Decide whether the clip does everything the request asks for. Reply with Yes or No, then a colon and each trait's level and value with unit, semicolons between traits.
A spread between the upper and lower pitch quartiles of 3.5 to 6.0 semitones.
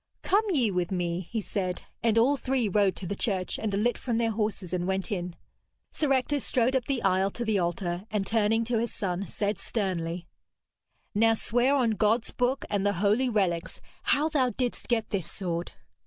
Yes: average, 4.4 semitones